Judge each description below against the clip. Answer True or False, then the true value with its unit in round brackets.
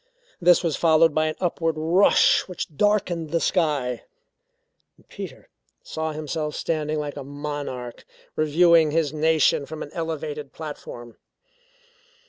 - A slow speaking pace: True (120 wpm)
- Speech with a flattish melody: True (2.0 semitones)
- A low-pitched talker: False (155 Hz)